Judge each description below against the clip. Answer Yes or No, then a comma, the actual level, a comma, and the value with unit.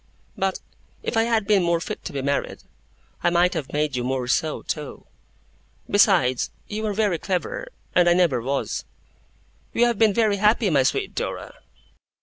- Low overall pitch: No, medium, 180 Hz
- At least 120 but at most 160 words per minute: No, average, 170 wpm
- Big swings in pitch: Yes, wide, 6.6 semitones